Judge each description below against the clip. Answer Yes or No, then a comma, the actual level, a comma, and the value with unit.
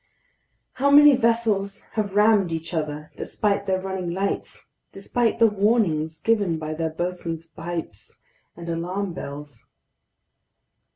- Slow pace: Yes, slow, 120 wpm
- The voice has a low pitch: No, medium, 185 Hz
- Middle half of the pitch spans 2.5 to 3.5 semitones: No, average, 4.3 semitones